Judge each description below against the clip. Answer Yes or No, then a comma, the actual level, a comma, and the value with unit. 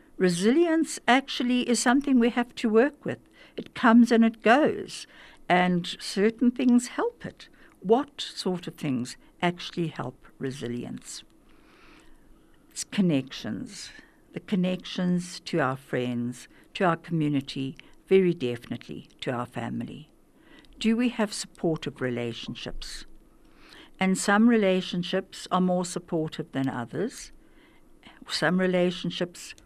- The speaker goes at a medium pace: No, slow, 115 wpm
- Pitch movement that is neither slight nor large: No, wide, 7.1 semitones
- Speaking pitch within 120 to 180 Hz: No, high, 190 Hz